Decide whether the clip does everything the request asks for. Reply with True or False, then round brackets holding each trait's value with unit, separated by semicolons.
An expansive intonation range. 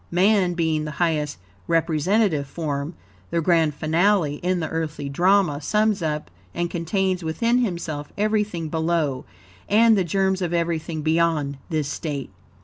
False (3.5 semitones)